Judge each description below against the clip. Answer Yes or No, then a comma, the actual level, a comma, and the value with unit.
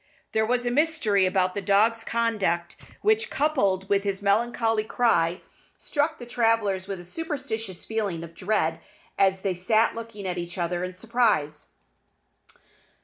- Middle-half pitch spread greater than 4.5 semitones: No, average, 3.9 semitones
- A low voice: No, high, 205 Hz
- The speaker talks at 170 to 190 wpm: No, average, 145 wpm